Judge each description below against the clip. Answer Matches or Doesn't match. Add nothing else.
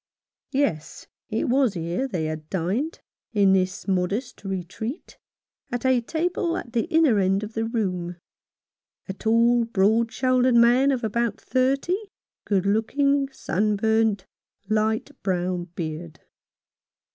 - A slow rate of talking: Matches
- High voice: Matches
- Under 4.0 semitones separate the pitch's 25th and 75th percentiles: Doesn't match